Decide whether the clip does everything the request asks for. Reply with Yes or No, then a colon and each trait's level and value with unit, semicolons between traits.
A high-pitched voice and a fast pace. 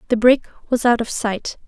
Yes: high, 235 Hz; fast, 215 wpm